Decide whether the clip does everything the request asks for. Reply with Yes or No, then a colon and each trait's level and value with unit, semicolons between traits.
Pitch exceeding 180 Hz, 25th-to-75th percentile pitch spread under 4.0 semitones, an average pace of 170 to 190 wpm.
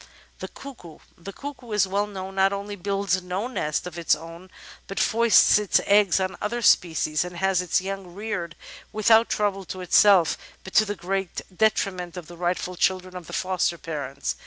Yes: high, 190 Hz; average, 2.7 semitones; average, 185 wpm